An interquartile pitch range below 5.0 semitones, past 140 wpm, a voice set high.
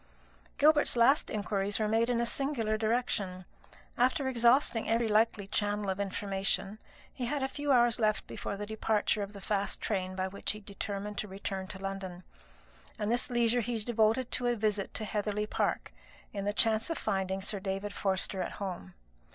Yes: average, 3.1 semitones; average, 185 wpm; high, 210 Hz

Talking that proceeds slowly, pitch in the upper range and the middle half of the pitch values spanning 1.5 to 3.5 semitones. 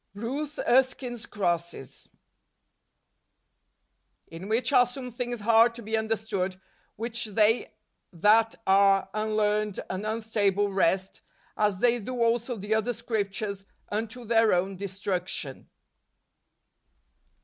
Yes: slow, 110 wpm; high, 215 Hz; average, 2.9 semitones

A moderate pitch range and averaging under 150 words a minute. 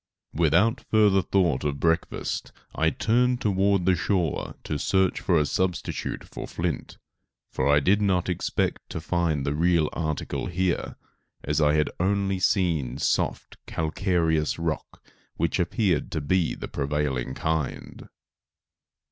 Yes: average, 3.8 semitones; slow, 135 wpm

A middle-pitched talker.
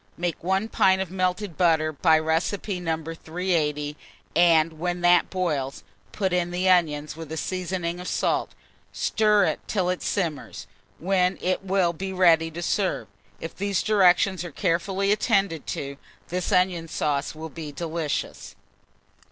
Yes: medium, 175 Hz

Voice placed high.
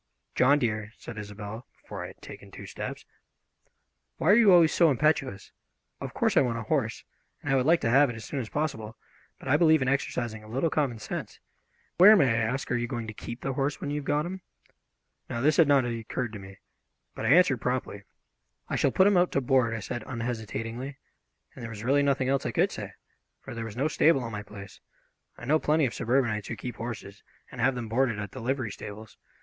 No: low, 125 Hz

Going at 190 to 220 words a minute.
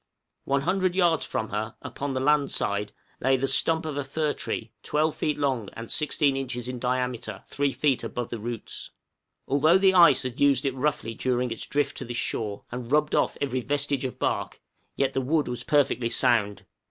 Yes: average, 200 wpm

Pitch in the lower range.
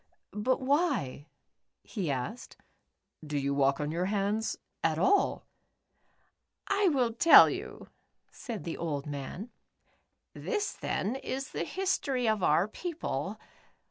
No: high, 215 Hz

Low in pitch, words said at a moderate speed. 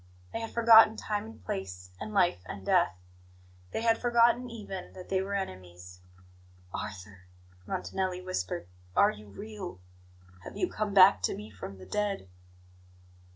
No: medium, 185 Hz; average, 150 wpm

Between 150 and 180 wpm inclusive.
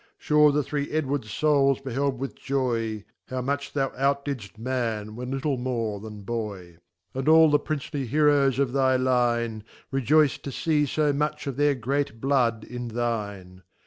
Yes: average, 165 wpm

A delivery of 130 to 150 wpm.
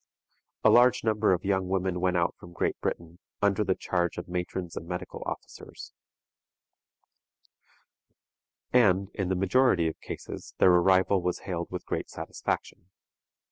Yes: average, 140 wpm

